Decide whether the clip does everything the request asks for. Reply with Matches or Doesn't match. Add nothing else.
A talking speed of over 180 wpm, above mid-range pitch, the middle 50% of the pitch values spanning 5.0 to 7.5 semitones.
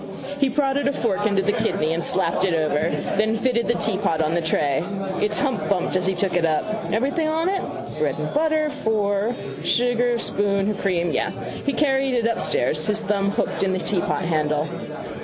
Matches